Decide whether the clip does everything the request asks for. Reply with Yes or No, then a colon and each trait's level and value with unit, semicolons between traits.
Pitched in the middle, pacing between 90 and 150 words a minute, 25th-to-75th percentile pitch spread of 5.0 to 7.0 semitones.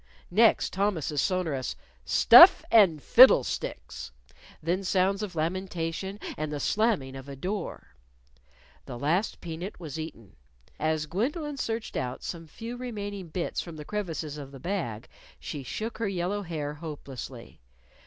Yes: medium, 170 Hz; average, 140 wpm; wide, 5.4 semitones